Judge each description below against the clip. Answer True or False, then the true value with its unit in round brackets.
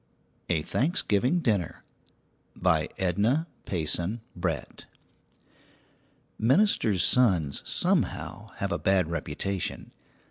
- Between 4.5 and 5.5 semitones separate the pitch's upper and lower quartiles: True (5.1 semitones)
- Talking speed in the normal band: False (80 wpm)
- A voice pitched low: True (95 Hz)